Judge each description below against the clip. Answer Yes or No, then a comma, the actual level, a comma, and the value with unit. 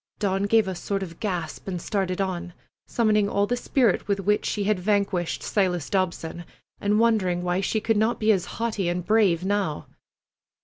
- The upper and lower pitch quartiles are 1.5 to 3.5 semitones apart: Yes, average, 2.9 semitones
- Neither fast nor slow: Yes, average, 185 wpm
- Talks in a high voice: Yes, high, 195 Hz